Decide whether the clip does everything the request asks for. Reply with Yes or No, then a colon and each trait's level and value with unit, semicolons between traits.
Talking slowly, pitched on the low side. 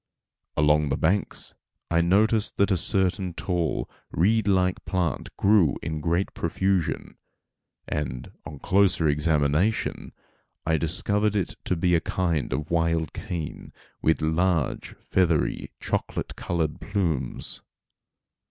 Yes: slow, 115 wpm; very low, 85 Hz